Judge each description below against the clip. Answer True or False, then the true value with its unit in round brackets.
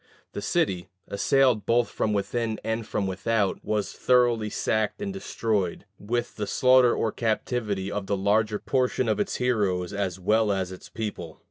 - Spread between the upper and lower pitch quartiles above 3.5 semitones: False (3.1 semitones)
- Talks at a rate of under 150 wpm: False (160 wpm)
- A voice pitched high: False (110 Hz)